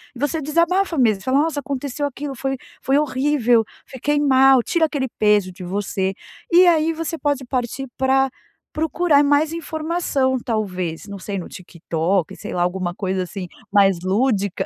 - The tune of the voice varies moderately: No, wide, 6.8 semitones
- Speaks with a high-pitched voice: Yes, very high, 265 Hz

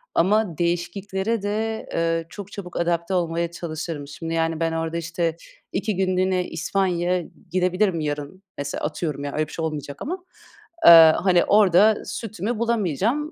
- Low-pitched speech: No, medium, 175 Hz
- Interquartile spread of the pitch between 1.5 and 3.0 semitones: No, average, 3.4 semitones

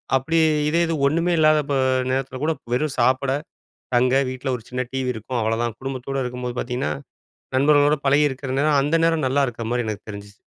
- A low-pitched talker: Yes, low, 130 Hz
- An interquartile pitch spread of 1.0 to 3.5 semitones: Yes, average, 2.9 semitones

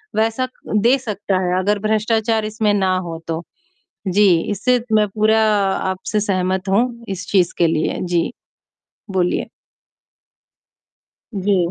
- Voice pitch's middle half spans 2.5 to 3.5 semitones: Yes, average, 2.8 semitones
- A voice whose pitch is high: Yes, high, 205 Hz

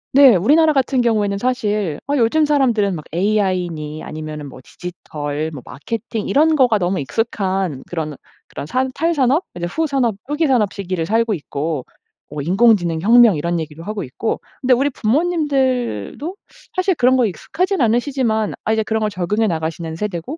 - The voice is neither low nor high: No, high, 215 Hz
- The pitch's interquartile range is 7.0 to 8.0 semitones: Yes, wide, 7.3 semitones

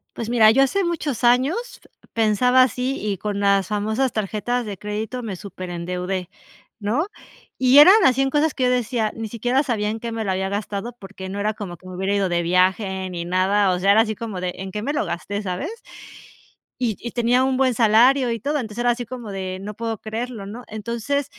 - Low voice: No, high, 220 Hz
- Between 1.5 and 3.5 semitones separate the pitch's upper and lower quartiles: No, average, 4.1 semitones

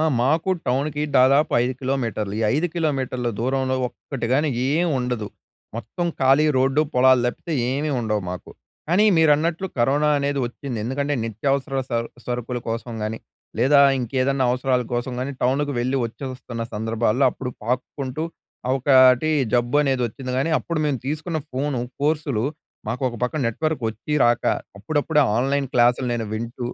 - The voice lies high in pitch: No, low, 130 Hz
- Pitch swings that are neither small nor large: Yes, average, 3.2 semitones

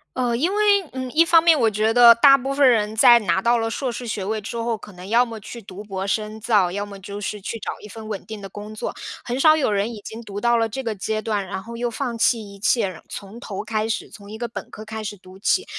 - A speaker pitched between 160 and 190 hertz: No, high, 220 Hz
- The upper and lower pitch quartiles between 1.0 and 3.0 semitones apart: Yes, average, 2.7 semitones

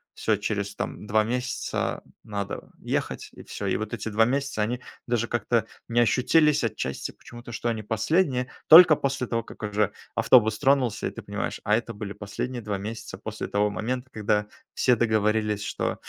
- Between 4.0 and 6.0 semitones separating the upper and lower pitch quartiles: No, average, 3.0 semitones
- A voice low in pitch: Yes, low, 110 Hz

